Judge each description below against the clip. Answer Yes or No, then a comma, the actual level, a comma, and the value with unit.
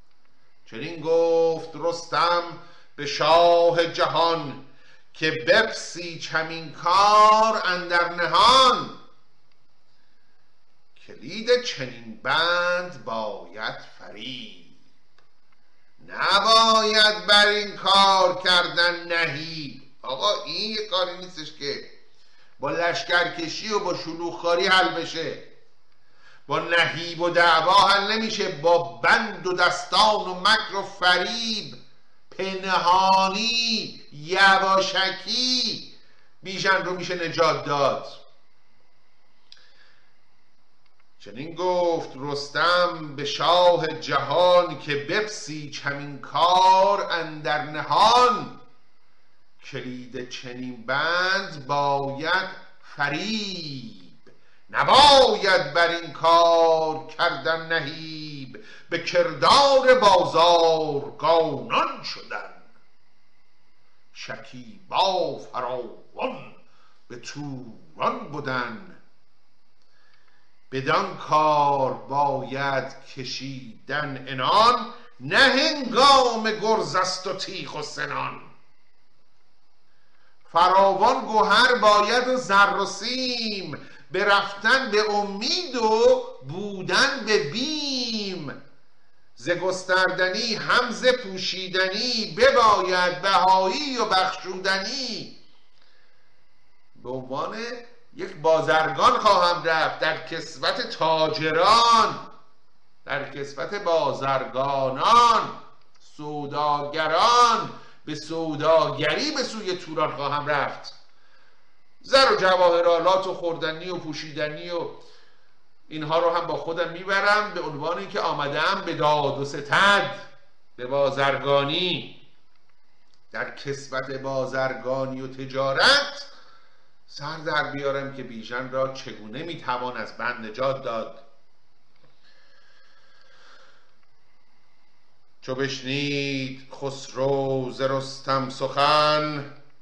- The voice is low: No, medium, 170 Hz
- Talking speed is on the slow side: Yes, slow, 85 wpm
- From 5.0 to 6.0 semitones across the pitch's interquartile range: Yes, wide, 5.5 semitones